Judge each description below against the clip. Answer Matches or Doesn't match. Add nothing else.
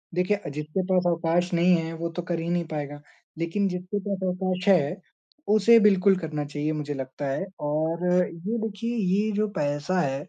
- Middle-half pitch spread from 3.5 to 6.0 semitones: Matches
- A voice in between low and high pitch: Matches